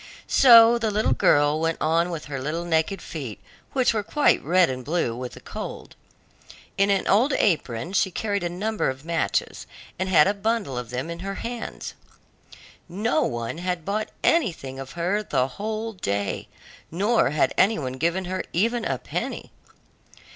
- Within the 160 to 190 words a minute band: Yes, average, 170 wpm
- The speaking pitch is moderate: Yes, medium, 180 Hz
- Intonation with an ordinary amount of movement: No, wide, 6.3 semitones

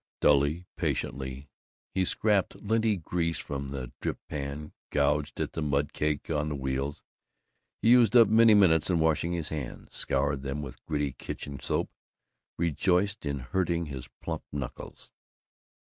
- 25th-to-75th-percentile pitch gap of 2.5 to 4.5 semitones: Yes, average, 4.1 semitones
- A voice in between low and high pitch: No, very low, 75 Hz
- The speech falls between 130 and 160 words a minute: Yes, average, 145 wpm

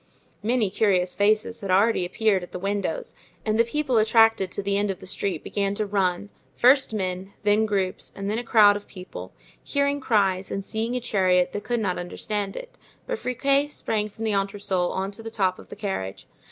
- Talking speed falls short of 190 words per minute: No, fast, 205 wpm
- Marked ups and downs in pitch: No, average, 2.8 semitones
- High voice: Yes, high, 205 Hz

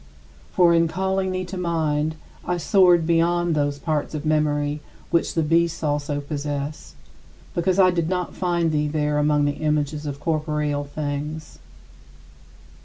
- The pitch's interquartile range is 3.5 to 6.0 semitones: No, narrow, 2.5 semitones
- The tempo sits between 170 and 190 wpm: No, average, 145 wpm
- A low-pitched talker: No, medium, 155 Hz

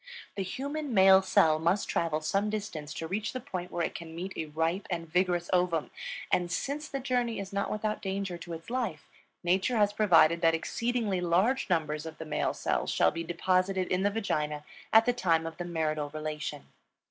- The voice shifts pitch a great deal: No, average, 4.2 semitones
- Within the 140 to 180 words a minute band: No, average, 195 wpm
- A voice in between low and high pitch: Yes, medium, 180 Hz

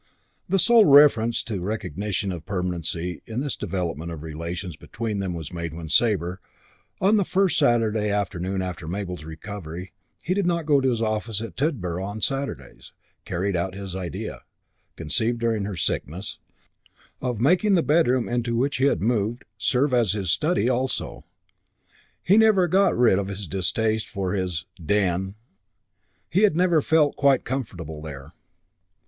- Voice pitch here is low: Yes, low, 105 Hz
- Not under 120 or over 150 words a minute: No, average, 160 wpm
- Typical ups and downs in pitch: No, wide, 6.7 semitones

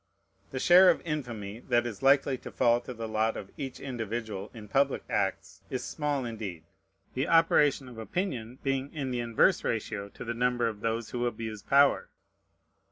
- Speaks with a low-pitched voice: Yes, low, 120 Hz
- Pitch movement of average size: Yes, average, 3.4 semitones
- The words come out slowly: No, average, 175 wpm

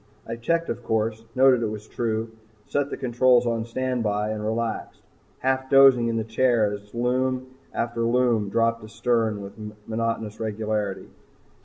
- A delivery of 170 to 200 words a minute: No, average, 150 wpm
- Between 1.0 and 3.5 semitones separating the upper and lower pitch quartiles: Yes, narrow, 2.5 semitones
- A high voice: No, low, 115 Hz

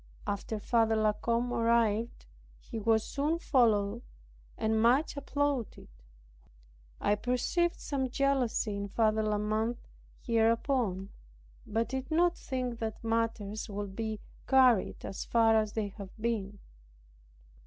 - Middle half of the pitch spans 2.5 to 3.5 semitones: Yes, average, 2.8 semitones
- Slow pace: Yes, slow, 120 wpm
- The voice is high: Yes, high, 225 Hz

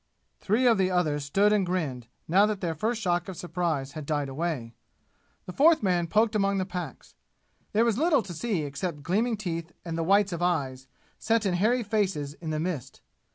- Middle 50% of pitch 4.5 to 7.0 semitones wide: Yes, average, 4.9 semitones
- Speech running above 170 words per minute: Yes, average, 200 wpm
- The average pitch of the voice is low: No, medium, 180 Hz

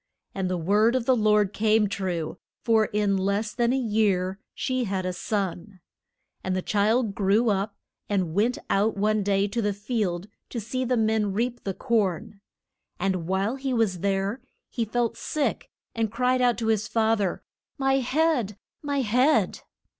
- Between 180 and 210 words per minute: No, average, 170 wpm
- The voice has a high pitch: Yes, high, 215 Hz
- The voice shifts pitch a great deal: No, average, 3.3 semitones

